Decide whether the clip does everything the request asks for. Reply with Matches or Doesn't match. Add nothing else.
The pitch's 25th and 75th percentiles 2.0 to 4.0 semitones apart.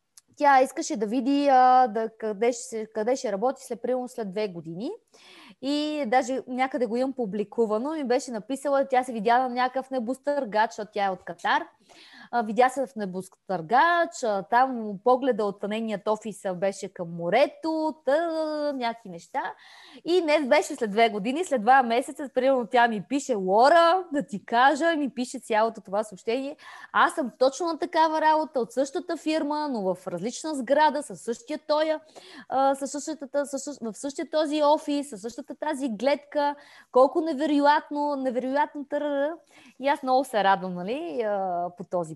Doesn't match